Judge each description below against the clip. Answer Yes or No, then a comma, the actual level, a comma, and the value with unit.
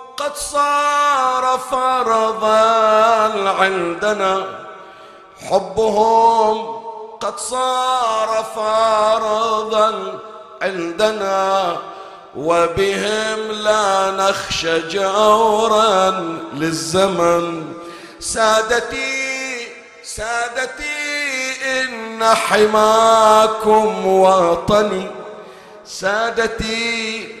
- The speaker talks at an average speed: No, slow, 45 wpm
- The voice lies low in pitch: No, high, 220 Hz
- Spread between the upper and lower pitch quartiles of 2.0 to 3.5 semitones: Yes, average, 2.8 semitones